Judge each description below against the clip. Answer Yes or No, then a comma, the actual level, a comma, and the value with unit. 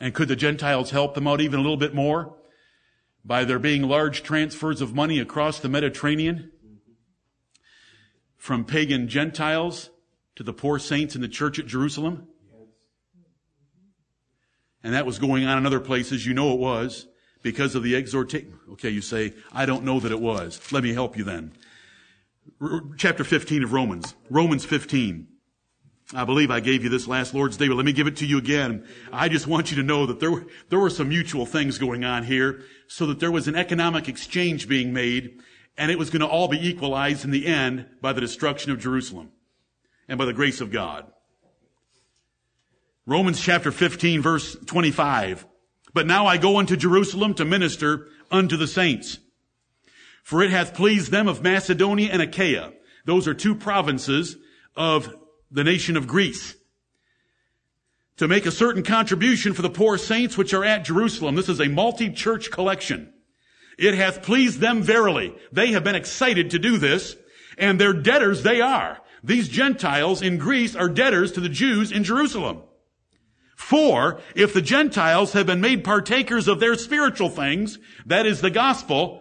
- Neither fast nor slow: Yes, average, 175 wpm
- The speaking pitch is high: No, medium, 155 Hz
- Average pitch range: No, wide, 5.9 semitones